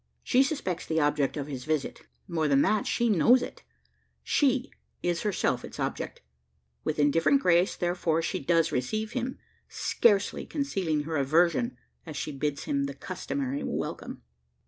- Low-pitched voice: No, medium, 165 Hz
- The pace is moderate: Yes, average, 150 wpm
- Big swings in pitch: Yes, wide, 6.6 semitones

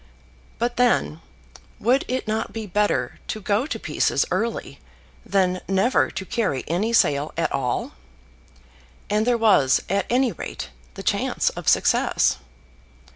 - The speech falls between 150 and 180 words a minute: No, slow, 135 wpm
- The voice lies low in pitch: No, high, 210 Hz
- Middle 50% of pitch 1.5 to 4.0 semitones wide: No, average, 4.5 semitones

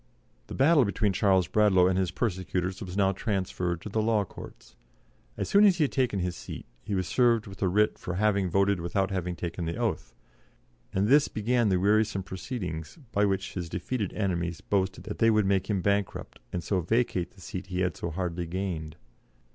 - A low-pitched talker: Yes, very low, 95 Hz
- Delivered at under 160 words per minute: No, average, 200 wpm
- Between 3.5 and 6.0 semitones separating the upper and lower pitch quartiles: No, average, 2.9 semitones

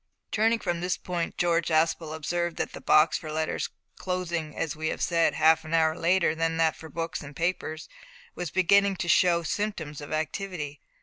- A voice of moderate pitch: Yes, medium, 165 Hz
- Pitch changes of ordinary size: No, narrow, 2.1 semitones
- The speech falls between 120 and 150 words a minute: No, average, 185 wpm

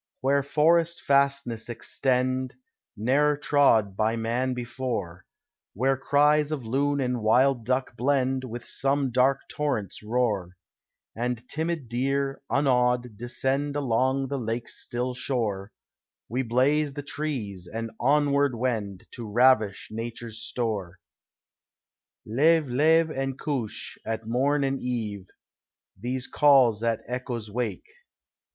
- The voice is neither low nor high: No, low, 125 Hz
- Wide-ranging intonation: No, average, 3.5 semitones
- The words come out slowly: Yes, slow, 120 wpm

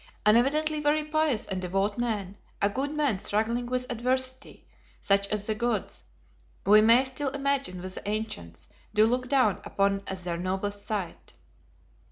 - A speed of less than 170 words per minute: Yes, average, 160 wpm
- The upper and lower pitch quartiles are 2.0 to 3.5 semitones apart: No, average, 4.7 semitones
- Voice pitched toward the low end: No, high, 220 Hz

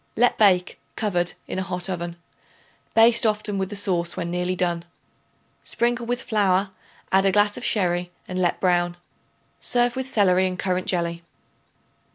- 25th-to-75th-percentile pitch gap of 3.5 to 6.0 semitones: No, average, 3.1 semitones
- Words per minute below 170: Yes, average, 160 wpm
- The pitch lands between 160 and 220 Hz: Yes, high, 190 Hz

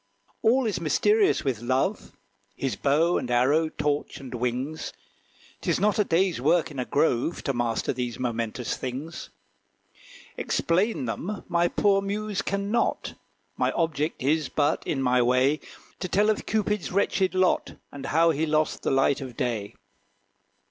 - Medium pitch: Yes, medium, 155 Hz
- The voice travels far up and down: Yes, wide, 6.7 semitones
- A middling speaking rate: Yes, average, 155 wpm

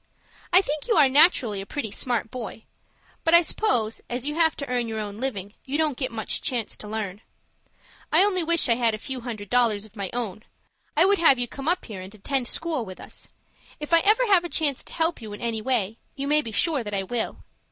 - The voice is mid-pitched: No, high, 245 Hz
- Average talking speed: No, fast, 235 wpm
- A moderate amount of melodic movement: No, wide, 6.1 semitones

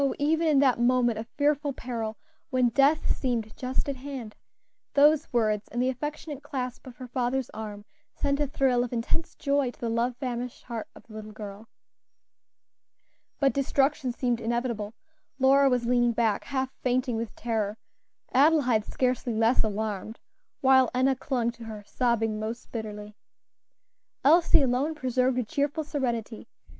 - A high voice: Yes, very high, 250 Hz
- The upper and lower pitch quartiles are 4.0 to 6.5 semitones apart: No, average, 3.2 semitones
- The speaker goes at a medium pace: Yes, average, 150 wpm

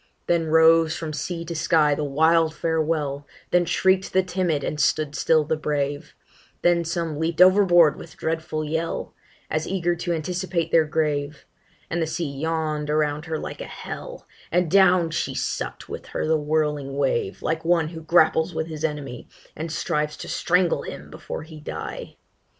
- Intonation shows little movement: Yes, narrow, 2.0 semitones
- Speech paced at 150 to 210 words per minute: Yes, average, 170 wpm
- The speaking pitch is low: No, medium, 160 Hz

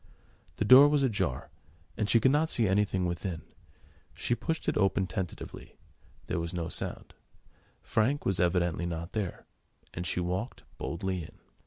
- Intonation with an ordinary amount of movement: Yes, average, 4.9 semitones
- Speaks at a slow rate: No, average, 155 wpm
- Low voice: Yes, very low, 95 Hz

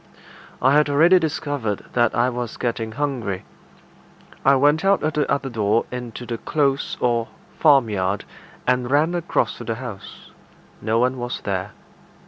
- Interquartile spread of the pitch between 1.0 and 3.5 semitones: No, average, 4.0 semitones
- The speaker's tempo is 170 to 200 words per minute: No, average, 150 wpm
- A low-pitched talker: Yes, low, 125 Hz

